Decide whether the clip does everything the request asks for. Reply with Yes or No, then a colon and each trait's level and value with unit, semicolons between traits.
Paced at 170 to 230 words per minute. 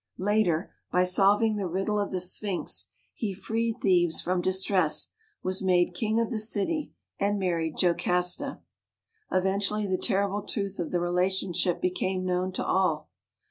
No: average, 150 wpm